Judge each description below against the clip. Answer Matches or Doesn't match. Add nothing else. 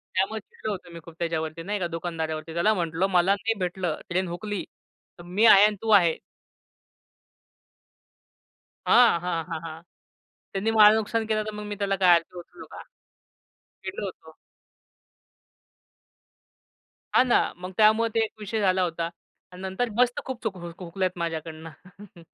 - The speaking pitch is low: Doesn't match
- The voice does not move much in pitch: Doesn't match